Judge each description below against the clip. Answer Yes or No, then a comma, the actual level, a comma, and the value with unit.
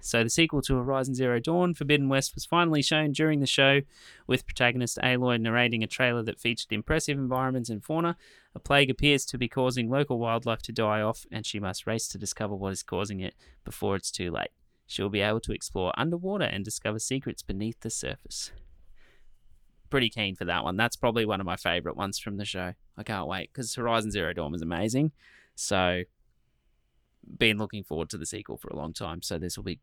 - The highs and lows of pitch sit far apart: No, average, 4.8 semitones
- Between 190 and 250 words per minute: Yes, fast, 205 wpm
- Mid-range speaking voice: No, low, 115 Hz